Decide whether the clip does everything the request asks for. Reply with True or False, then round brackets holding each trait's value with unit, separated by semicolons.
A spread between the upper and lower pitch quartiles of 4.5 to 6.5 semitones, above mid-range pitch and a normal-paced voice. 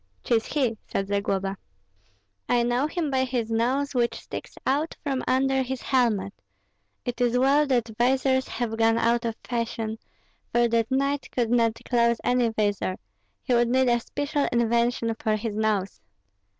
False (2.6 semitones; 240 Hz; 160 wpm)